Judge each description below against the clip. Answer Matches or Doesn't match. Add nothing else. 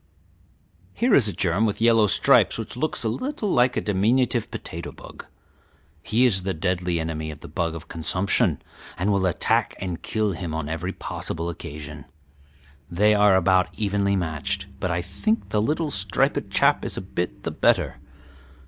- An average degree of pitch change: Matches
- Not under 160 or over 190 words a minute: Matches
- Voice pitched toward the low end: Matches